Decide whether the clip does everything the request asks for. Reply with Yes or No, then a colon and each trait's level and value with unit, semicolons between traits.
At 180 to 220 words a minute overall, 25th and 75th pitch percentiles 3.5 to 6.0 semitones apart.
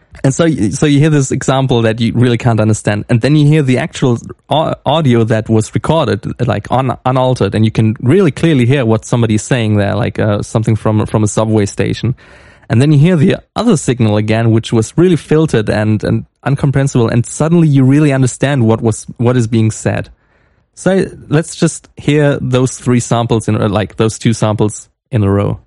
Yes: average, 195 wpm; average, 4.3 semitones